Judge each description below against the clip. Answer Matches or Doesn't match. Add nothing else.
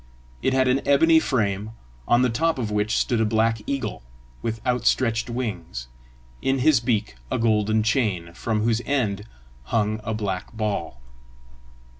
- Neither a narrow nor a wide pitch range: Matches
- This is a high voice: Doesn't match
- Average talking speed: Matches